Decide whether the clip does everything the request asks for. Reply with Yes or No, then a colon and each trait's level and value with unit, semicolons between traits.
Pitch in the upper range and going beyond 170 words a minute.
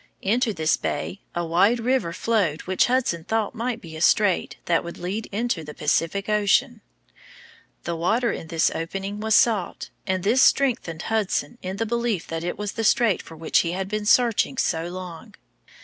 Yes: high, 200 Hz; average, 180 wpm